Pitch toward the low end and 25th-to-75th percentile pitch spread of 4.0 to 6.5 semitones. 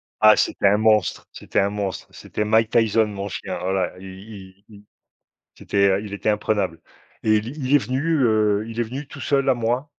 No: low, 110 Hz; narrow, 2.5 semitones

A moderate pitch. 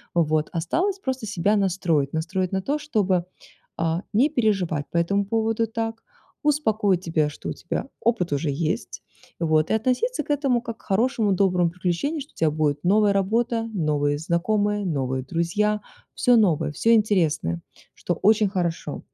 No: high, 195 Hz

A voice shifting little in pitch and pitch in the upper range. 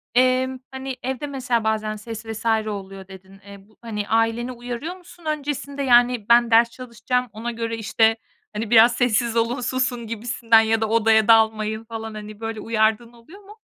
Yes: narrow, 2.2 semitones; high, 230 Hz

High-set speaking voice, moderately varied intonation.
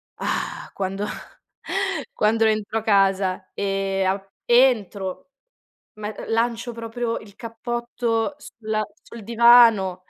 Yes: high, 220 Hz; average, 3.1 semitones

